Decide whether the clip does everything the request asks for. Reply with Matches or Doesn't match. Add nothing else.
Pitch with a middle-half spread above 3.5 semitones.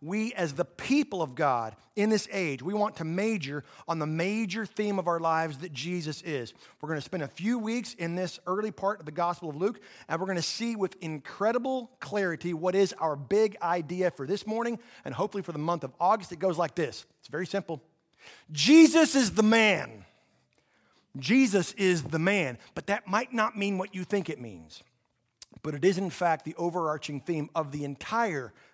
Matches